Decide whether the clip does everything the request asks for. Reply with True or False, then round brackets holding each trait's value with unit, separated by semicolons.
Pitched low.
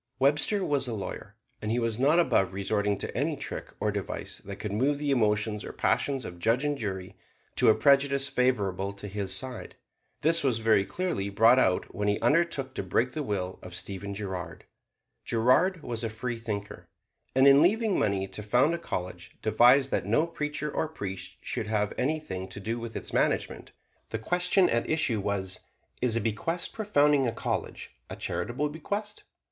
True (115 Hz)